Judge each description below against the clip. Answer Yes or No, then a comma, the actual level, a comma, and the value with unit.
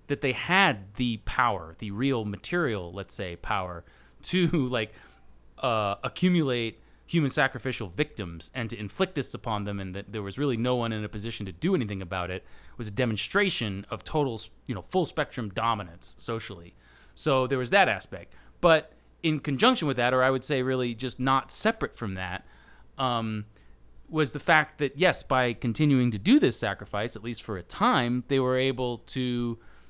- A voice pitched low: Yes, low, 120 Hz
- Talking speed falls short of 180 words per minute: No, average, 185 wpm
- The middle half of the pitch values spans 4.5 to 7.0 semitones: Yes, average, 5.0 semitones